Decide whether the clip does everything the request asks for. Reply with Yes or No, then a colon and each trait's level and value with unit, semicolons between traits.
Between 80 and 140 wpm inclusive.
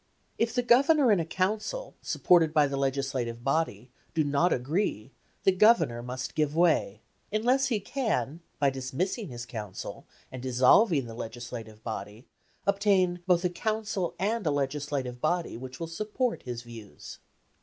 No: average, 150 wpm